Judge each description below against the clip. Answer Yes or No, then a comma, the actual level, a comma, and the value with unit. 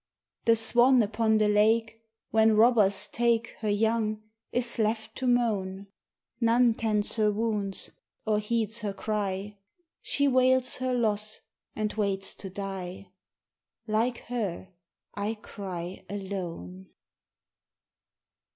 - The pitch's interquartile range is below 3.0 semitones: Yes, narrow, 2.5 semitones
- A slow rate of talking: Yes, slow, 115 wpm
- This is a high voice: Yes, high, 215 Hz